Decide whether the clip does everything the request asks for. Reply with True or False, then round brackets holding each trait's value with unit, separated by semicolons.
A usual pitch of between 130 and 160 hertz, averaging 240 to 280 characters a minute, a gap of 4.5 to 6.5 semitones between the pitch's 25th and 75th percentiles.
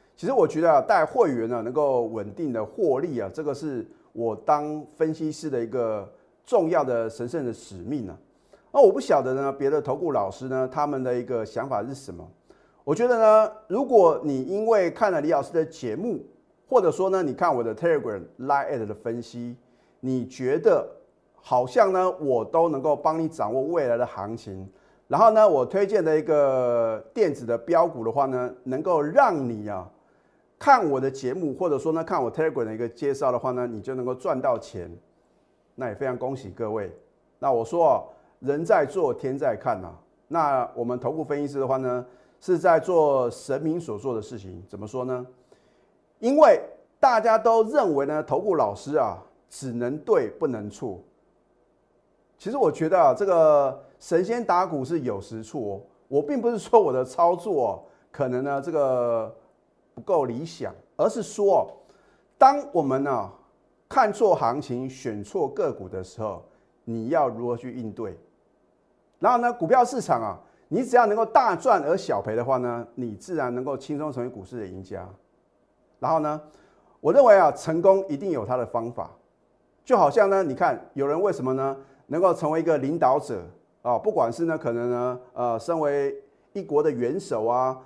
True (135 Hz; 270 characters per minute; 5.5 semitones)